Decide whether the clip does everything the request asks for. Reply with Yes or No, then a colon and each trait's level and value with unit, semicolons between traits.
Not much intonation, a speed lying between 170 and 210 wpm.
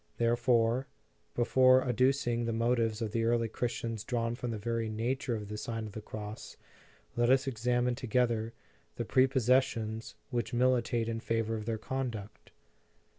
No: narrow, 1.8 semitones; average, 150 wpm